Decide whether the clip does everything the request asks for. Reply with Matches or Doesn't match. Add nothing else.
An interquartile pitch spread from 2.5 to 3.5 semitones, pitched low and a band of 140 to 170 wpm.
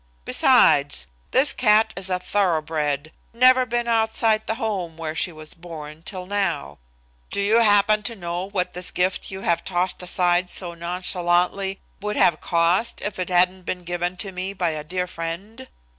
Doesn't match